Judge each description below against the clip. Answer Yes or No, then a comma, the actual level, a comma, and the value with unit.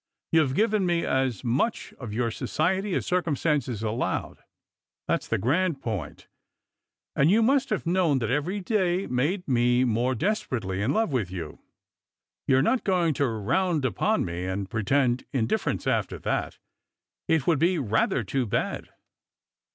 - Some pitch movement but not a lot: No, wide, 7.5 semitones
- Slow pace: No, average, 155 wpm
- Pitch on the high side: No, low, 135 Hz